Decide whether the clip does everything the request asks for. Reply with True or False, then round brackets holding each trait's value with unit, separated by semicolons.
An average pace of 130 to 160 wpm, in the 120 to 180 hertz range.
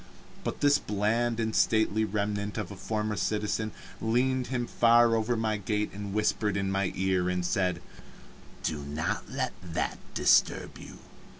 False (155 wpm; 105 Hz)